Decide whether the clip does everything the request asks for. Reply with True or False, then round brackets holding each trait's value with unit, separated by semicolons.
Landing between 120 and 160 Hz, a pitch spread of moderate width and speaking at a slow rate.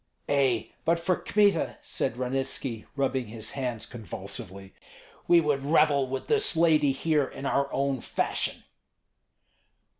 True (135 Hz; 3.7 semitones; 125 wpm)